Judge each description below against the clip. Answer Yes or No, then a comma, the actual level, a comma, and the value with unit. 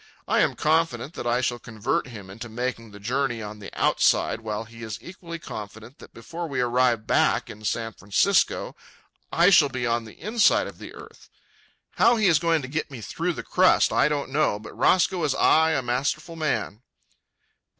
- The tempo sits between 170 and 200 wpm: Yes, average, 190 wpm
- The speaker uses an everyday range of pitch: No, wide, 6.0 semitones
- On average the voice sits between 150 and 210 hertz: No, low, 125 Hz